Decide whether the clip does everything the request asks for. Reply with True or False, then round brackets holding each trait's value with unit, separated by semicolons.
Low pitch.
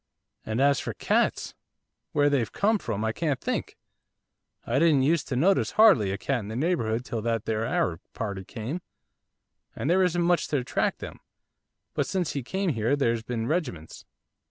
True (130 Hz)